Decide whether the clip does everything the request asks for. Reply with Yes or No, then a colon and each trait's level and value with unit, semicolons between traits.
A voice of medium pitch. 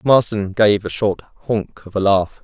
No: low, 100 Hz